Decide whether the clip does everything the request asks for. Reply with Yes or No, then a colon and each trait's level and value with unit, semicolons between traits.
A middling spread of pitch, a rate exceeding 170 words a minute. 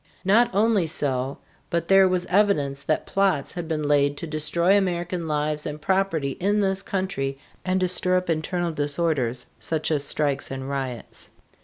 No: average, 4.5 semitones; average, 165 wpm